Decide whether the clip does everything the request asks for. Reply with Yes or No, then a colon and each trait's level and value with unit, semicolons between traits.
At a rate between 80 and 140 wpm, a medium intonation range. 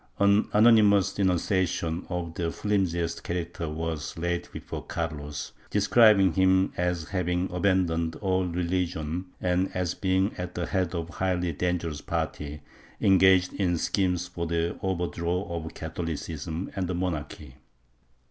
No: slow, 135 wpm; narrow, 2.1 semitones